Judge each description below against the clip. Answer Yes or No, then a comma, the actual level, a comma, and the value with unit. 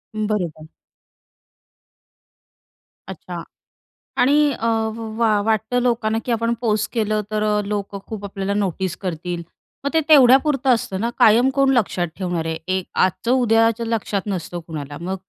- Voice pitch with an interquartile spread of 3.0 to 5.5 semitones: Yes, average, 3.7 semitones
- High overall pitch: Yes, high, 215 Hz